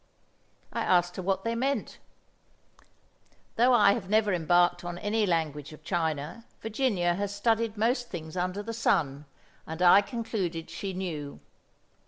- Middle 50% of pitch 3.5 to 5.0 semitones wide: Yes, average, 4.5 semitones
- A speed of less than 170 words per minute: Yes, average, 145 wpm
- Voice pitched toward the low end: No, high, 190 Hz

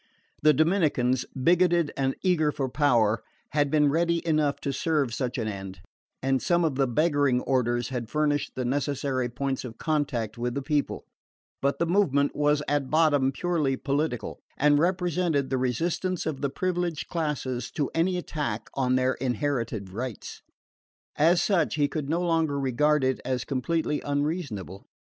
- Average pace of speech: Yes, average, 160 wpm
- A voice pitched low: No, medium, 145 Hz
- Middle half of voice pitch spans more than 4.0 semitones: No, average, 3.6 semitones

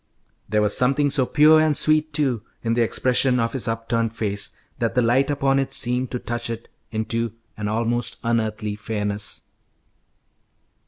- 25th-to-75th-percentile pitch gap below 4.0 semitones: Yes, average, 3.5 semitones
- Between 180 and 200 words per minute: No, average, 160 wpm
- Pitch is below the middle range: Yes, low, 120 Hz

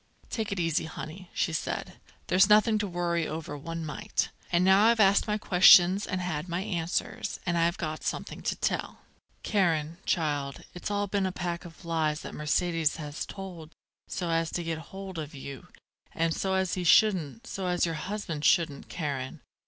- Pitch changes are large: No, average, 3.1 semitones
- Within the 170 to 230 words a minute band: Yes, average, 185 wpm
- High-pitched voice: No, medium, 175 Hz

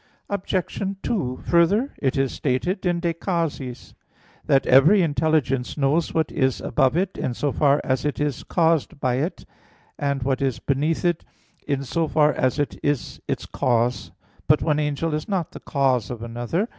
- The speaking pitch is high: No, medium, 145 Hz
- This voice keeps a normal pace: Yes, average, 170 wpm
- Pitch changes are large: No, average, 4.1 semitones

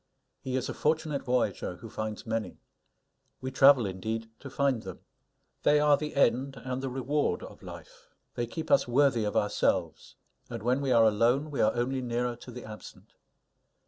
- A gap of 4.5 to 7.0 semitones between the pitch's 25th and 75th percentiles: No, average, 3.5 semitones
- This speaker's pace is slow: No, average, 175 wpm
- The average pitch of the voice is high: No, low, 125 Hz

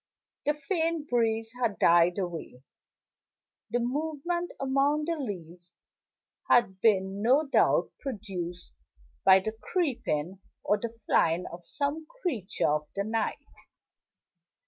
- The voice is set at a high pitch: Yes, high, 225 Hz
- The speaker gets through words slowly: Yes, slow, 115 wpm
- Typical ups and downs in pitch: No, wide, 7.6 semitones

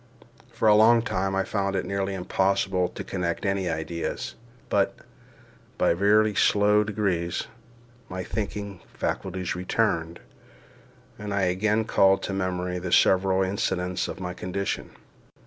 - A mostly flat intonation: Yes, narrow, 2.1 semitones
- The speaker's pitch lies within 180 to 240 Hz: No, very low, 95 Hz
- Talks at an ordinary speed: No, slow, 130 wpm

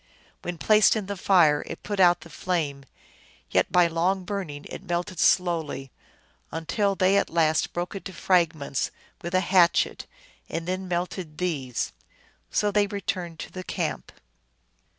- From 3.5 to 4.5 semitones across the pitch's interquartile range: No, narrow, 2.6 semitones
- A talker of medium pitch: Yes, medium, 175 Hz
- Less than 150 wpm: No, average, 155 wpm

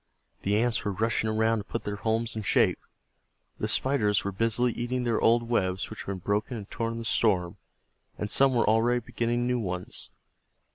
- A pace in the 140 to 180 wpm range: No, average, 195 wpm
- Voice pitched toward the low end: Yes, low, 110 Hz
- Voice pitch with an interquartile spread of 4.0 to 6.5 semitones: No, narrow, 2.5 semitones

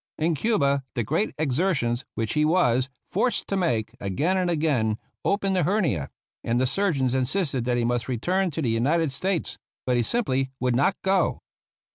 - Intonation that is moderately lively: No, wide, 7.0 semitones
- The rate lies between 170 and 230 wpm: Yes, average, 175 wpm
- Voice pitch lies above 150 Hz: No, medium, 140 Hz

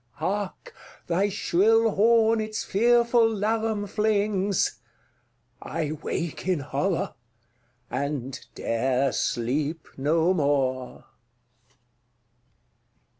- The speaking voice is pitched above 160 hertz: Yes, high, 190 Hz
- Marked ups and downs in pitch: Yes, wide, 7.1 semitones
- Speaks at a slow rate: Yes, slow, 75 wpm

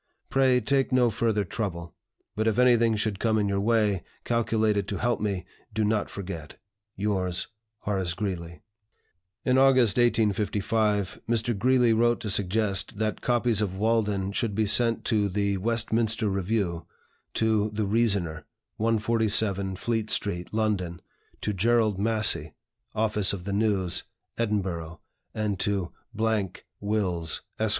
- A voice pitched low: Yes, low, 105 Hz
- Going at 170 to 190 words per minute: No, slow, 135 wpm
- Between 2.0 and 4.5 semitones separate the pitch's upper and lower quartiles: Yes, narrow, 2.6 semitones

